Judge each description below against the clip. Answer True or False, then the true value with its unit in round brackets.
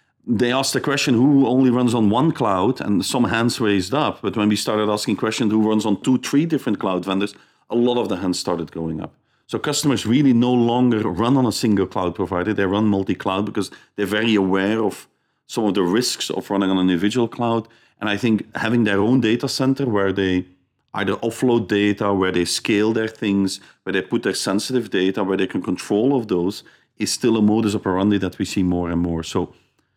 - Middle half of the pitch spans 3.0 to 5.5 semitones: True (3.7 semitones)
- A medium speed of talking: False (215 wpm)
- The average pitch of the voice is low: True (105 Hz)